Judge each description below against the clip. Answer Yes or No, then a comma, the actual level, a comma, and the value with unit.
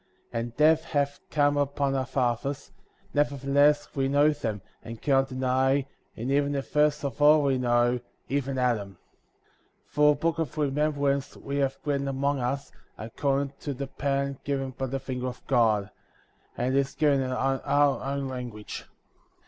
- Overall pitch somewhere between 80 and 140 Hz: Yes, low, 135 Hz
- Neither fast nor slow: Yes, average, 170 wpm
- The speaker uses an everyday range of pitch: No, narrow, 1.8 semitones